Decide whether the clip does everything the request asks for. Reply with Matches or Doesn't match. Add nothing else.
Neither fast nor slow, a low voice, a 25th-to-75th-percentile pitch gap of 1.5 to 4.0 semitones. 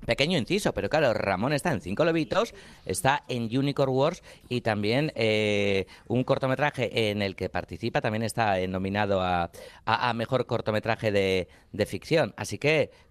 Doesn't match